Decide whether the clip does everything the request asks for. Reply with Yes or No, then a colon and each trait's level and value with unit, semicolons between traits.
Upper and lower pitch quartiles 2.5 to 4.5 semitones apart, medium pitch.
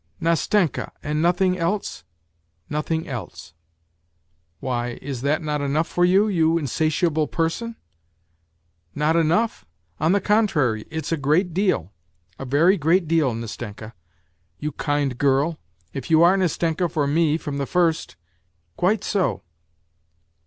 No: wide, 5.4 semitones; medium, 155 Hz